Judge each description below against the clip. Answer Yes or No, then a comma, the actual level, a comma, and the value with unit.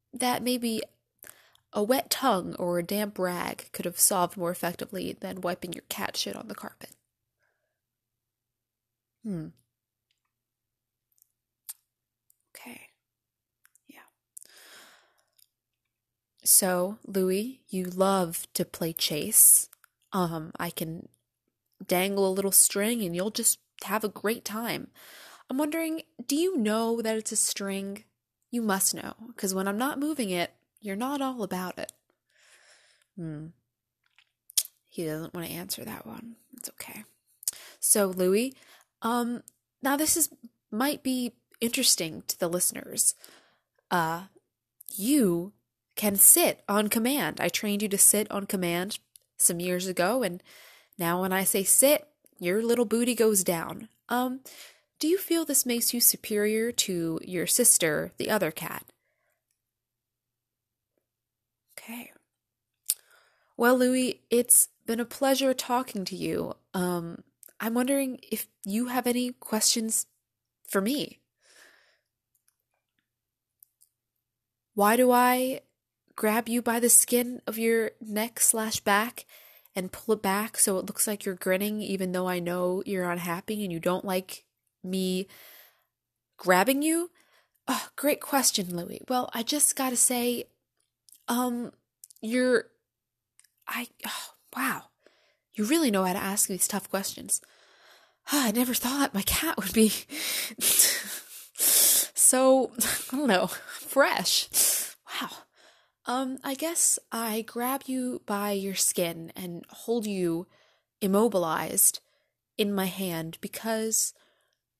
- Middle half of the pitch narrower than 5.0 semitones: No, wide, 5.5 semitones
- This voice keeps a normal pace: No, slow, 125 wpm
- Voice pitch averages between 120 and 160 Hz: No, high, 205 Hz